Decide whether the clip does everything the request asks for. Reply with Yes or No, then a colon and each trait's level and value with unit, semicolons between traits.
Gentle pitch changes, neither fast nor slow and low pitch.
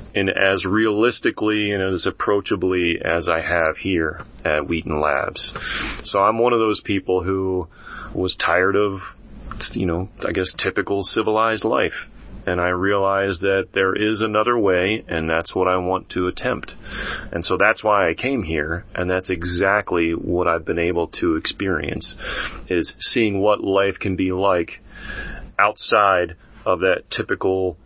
Yes: narrow, 2.3 semitones; average, 155 wpm; very low, 95 Hz